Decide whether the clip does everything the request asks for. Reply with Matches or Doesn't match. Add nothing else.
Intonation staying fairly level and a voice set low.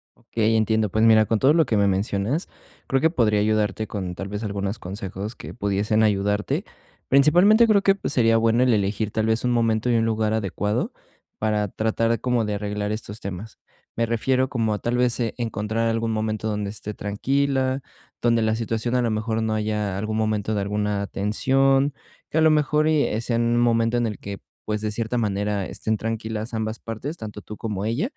Matches